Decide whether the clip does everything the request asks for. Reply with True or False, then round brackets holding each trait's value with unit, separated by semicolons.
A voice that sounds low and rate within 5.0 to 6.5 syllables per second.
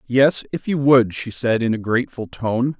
False (125 Hz; 4.6 syllables/s)